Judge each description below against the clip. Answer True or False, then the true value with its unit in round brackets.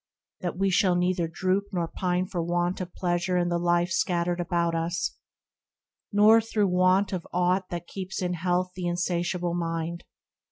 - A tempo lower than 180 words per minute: True (165 wpm)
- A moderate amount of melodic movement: False (1.2 semitones)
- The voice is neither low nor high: True (180 Hz)